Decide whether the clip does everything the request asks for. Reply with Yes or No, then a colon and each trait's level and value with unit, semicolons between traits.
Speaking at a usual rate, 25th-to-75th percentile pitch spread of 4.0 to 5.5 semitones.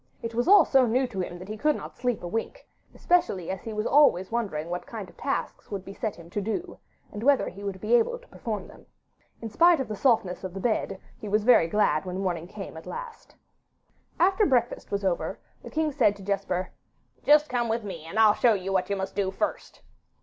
No: fast, 230 wpm; average, 4.9 semitones